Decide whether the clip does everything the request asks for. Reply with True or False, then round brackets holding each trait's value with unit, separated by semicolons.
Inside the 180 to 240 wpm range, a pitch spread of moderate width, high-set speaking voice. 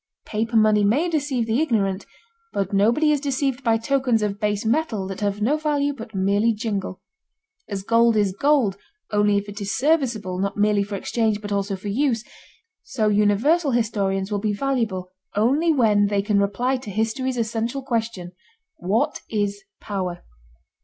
False (165 wpm; 3.8 semitones; 215 Hz)